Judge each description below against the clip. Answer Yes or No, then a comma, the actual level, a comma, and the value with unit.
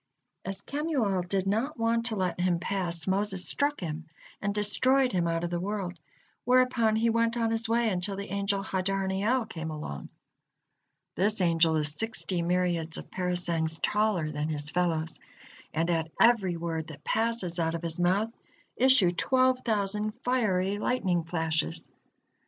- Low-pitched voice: No, high, 190 Hz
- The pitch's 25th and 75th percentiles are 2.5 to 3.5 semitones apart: No, average, 4.8 semitones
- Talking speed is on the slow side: No, average, 155 wpm